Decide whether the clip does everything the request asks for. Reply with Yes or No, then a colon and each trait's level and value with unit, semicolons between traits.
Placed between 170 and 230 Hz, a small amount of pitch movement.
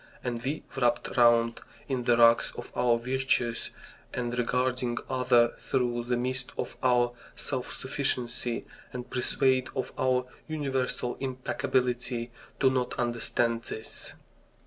No: low, 125 Hz; narrow, 1.4 semitones